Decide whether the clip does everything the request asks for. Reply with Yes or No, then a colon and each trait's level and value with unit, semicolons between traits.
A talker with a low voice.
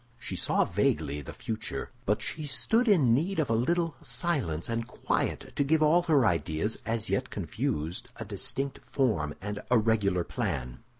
Yes: low, 115 Hz